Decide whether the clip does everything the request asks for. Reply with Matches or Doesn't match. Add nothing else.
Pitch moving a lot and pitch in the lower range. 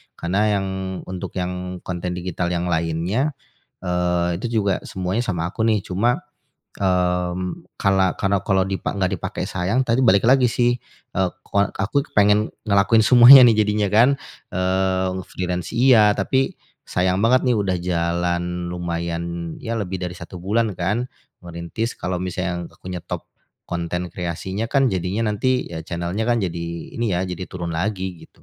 Doesn't match